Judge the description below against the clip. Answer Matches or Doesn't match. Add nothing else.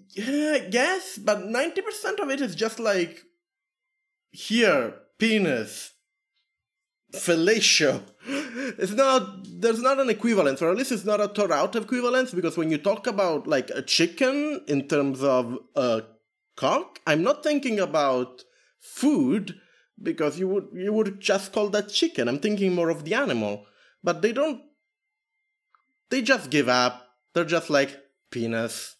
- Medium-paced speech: Matches